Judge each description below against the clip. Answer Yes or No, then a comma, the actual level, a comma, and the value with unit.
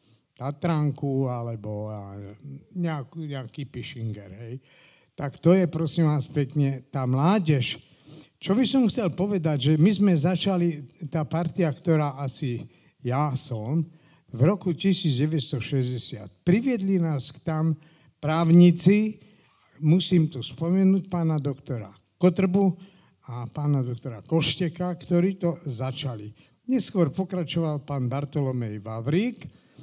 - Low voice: No, medium, 155 Hz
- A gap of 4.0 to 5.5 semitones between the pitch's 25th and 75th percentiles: Yes, average, 4.7 semitones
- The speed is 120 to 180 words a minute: No, slow, 110 wpm